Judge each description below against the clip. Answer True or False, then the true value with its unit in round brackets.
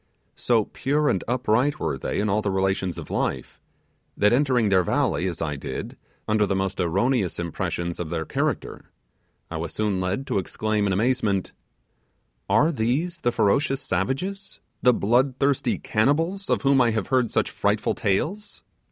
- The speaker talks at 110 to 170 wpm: True (165 wpm)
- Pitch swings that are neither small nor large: False (6.0 semitones)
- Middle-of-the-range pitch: False (110 Hz)